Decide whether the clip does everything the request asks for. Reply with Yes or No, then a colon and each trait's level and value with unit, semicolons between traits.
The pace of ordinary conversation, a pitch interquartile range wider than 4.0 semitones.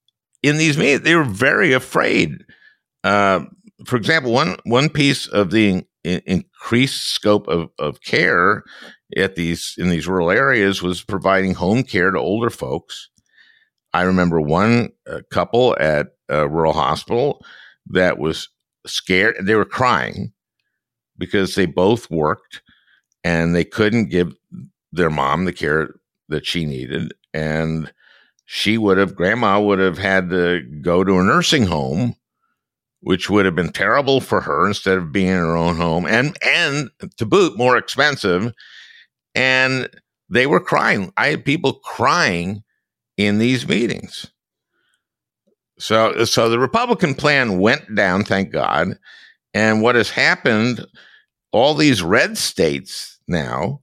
Yes: average, 145 wpm; average, 4.7 semitones